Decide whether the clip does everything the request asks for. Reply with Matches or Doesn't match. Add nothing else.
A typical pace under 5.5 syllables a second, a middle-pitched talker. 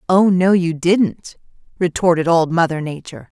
Matches